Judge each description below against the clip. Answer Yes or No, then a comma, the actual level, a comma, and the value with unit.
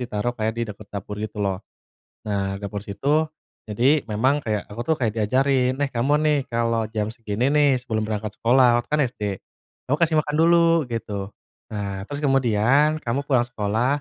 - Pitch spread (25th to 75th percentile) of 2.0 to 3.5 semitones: No, average, 4.1 semitones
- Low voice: Yes, low, 115 Hz